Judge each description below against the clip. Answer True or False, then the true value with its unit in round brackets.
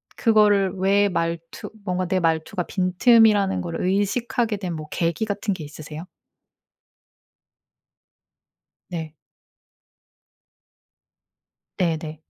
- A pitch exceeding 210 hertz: False (185 Hz)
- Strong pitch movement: False (3.5 semitones)